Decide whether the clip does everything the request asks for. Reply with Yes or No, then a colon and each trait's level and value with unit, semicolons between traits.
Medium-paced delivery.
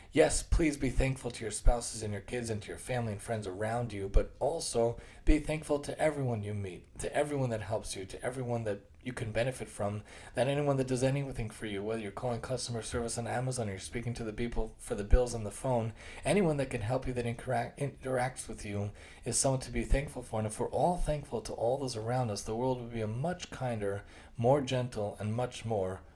No: fast, 235 wpm